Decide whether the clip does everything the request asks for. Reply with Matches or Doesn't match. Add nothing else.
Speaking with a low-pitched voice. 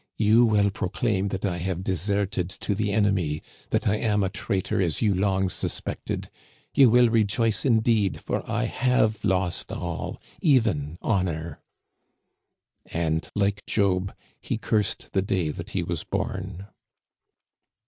Matches